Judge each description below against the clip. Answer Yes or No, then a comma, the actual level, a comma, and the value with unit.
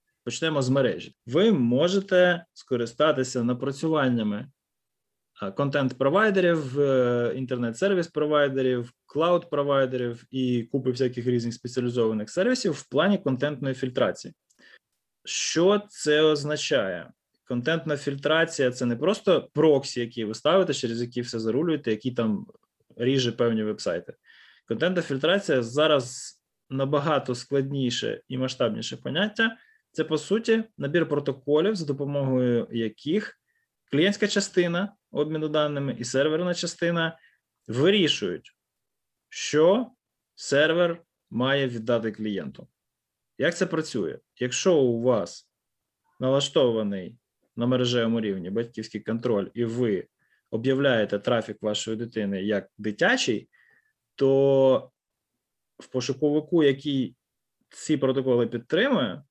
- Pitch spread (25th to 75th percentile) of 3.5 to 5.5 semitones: Yes, average, 4.8 semitones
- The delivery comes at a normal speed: No, slow, 100 wpm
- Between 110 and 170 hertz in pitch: Yes, low, 135 Hz